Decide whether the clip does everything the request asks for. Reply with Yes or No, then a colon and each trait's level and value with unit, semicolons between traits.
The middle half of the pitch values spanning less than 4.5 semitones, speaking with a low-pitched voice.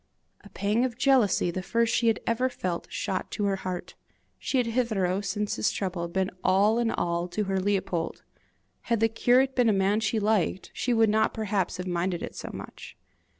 No: average, 3.5 semitones; high, 205 Hz